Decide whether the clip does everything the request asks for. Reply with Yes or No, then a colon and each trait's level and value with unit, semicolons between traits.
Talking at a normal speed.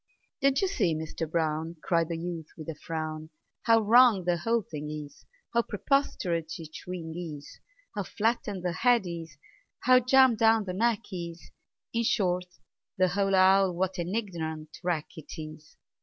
Yes: average, 165 wpm